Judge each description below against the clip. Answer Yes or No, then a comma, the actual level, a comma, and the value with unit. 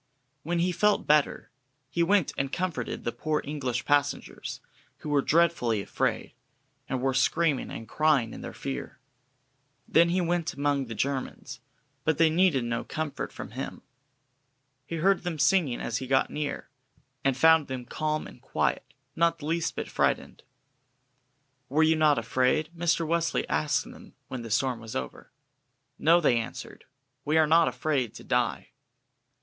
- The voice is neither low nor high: Yes, medium, 150 Hz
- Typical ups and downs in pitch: Yes, average, 4.1 semitones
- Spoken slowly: No, average, 160 wpm